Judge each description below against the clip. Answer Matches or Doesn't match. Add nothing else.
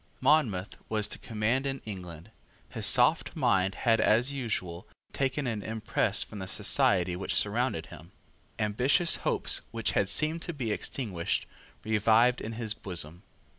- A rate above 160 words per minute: Doesn't match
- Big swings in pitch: Doesn't match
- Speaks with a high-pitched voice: Doesn't match